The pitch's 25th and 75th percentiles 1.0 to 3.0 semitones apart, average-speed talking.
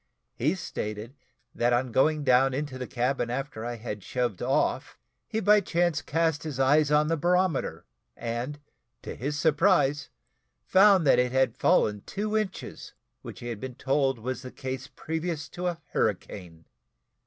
No: average, 4.9 semitones; average, 160 wpm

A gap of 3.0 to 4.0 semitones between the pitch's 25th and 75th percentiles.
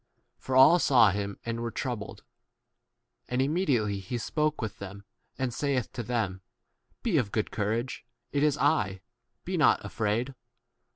No: average, 4.6 semitones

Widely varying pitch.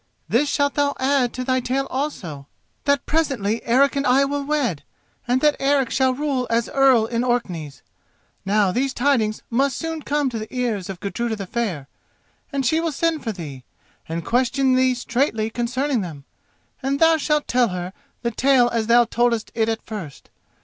No: average, 4.0 semitones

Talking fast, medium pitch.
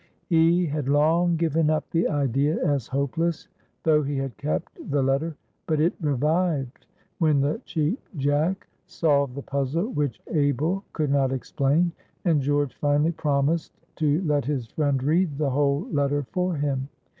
No: average, 155 wpm; medium, 145 Hz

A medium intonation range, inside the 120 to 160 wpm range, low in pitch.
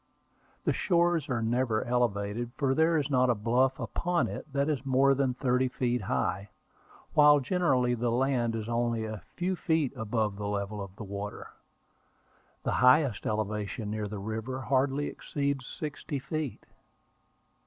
Yes: average, 4.4 semitones; average, 155 wpm; low, 125 Hz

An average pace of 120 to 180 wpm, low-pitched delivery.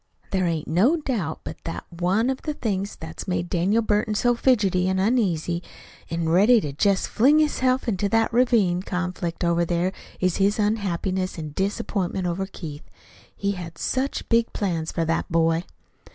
No: average, 165 wpm; high, 190 Hz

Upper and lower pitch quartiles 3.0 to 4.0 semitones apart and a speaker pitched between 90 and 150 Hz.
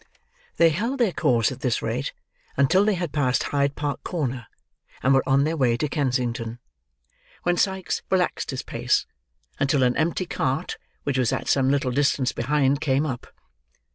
Yes: average, 3.7 semitones; medium, 140 Hz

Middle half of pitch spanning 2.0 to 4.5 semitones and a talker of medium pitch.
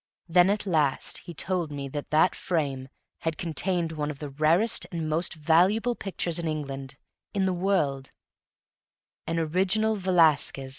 Yes: average, 3.8 semitones; medium, 165 Hz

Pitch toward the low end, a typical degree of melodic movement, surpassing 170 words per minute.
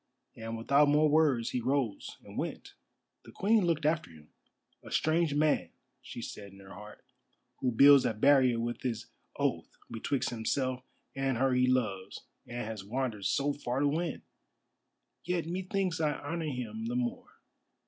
No: low, 130 Hz; average, 4.7 semitones; average, 160 wpm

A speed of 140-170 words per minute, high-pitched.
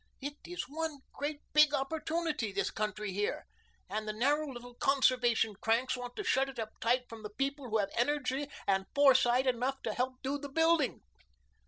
No: average, 180 wpm; very high, 260 Hz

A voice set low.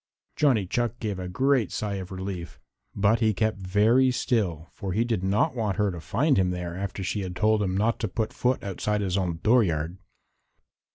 Yes: low, 100 Hz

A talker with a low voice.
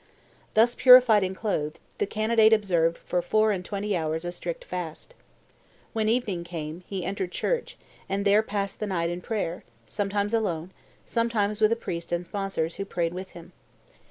No: high, 195 Hz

